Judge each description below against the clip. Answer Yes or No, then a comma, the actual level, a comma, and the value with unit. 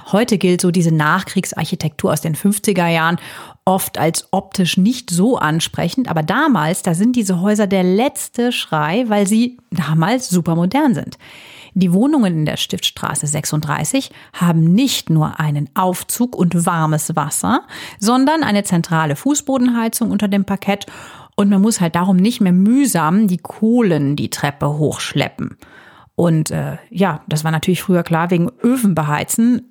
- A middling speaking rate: Yes, average, 150 wpm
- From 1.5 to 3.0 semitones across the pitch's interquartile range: No, average, 5.1 semitones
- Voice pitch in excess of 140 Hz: Yes, medium, 185 Hz